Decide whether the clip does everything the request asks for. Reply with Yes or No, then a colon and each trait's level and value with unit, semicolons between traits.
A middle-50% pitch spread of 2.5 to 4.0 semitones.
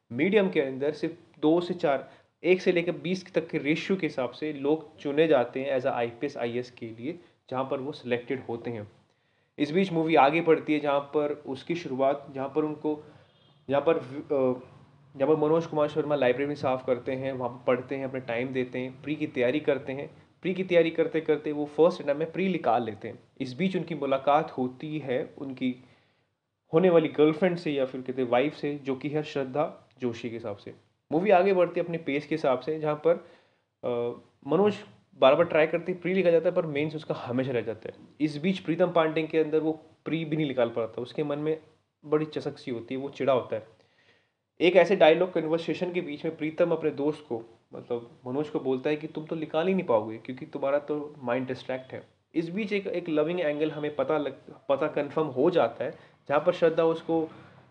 Yes: average, 3.7 semitones